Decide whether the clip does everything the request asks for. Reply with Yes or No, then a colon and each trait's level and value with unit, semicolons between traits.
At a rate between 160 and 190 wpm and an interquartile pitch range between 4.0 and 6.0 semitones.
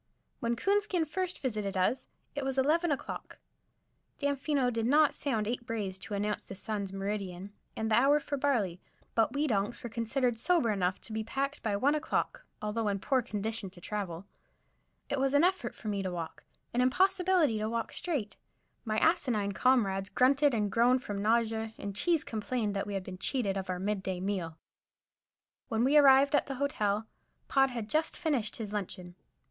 Yes: average, 185 wpm; wide, 5.5 semitones